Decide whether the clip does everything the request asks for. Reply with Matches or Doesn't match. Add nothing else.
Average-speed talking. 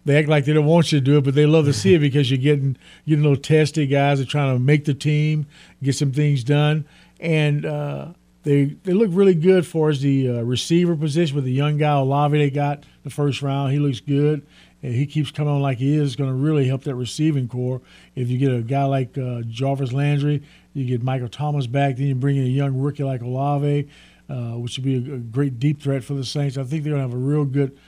Doesn't match